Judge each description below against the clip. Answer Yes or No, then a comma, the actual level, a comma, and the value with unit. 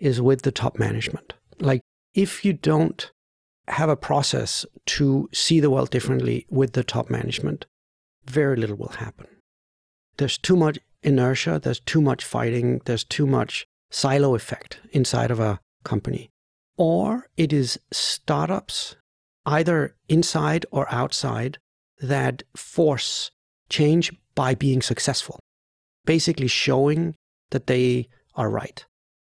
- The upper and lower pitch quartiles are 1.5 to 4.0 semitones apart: No, average, 4.8 semitones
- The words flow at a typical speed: No, slow, 125 wpm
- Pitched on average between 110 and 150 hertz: Yes, low, 135 Hz